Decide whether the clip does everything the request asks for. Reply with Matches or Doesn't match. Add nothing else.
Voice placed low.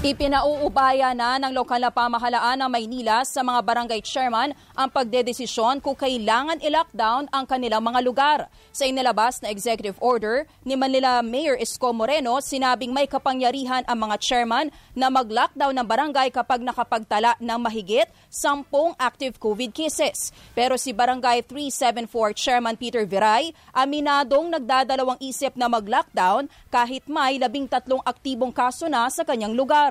Doesn't match